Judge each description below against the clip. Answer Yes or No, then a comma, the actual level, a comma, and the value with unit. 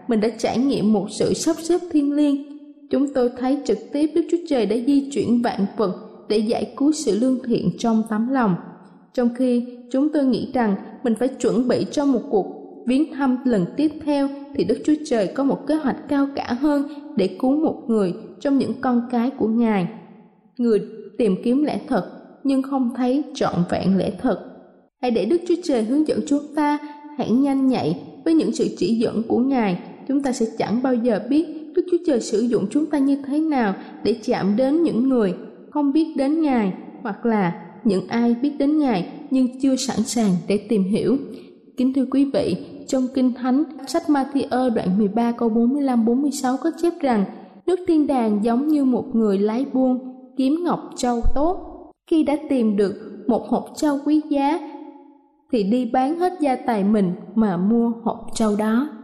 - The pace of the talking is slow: No, average, 195 wpm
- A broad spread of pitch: No, average, 4.3 semitones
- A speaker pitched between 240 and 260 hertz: Yes, very high, 255 Hz